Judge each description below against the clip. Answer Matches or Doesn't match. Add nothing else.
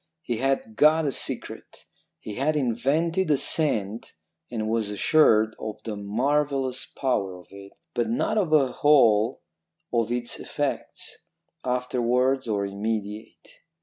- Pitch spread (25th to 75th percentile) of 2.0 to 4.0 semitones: Doesn't match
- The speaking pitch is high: Doesn't match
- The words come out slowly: Matches